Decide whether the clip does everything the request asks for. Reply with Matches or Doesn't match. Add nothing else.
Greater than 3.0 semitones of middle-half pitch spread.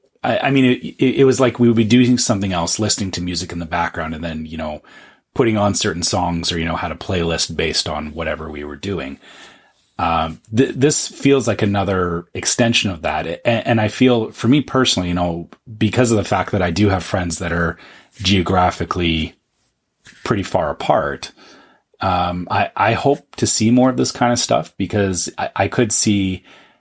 Matches